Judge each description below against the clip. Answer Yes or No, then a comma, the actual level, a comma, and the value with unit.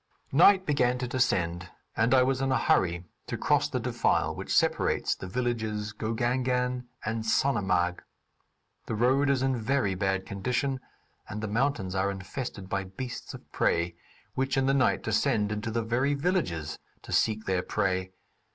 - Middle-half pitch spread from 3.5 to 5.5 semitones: Yes, average, 5.2 semitones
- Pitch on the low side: Yes, low, 115 Hz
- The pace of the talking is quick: No, average, 160 wpm